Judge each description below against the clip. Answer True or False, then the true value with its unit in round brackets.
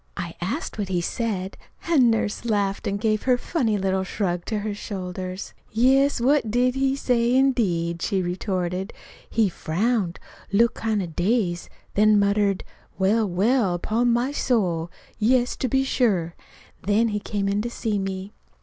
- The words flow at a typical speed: True (160 wpm)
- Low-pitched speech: False (210 Hz)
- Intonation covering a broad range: False (4.1 semitones)